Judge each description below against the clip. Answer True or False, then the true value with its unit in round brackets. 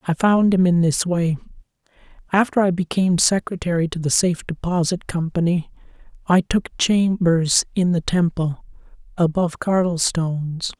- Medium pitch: True (175 Hz)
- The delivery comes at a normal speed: False (130 wpm)